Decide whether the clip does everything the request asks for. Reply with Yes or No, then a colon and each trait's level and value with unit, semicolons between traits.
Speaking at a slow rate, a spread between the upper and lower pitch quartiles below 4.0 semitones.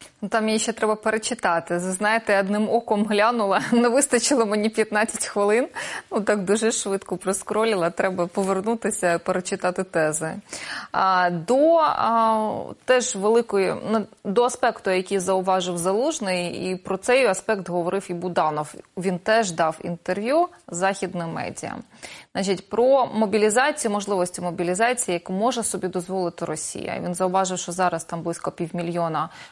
No: average, 130 wpm; average, 3.5 semitones